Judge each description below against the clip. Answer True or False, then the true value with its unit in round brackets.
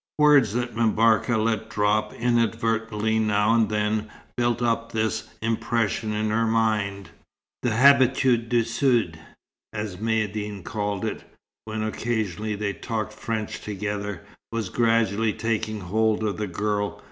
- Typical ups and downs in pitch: False (1.6 semitones)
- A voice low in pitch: True (110 Hz)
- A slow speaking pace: True (130 wpm)